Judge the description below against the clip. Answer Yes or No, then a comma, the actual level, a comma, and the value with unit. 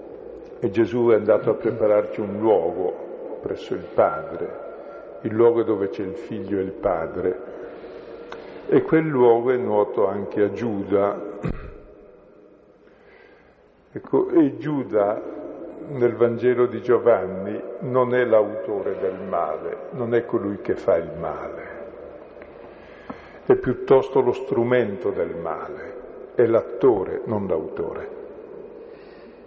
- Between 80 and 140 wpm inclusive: Yes, slow, 115 wpm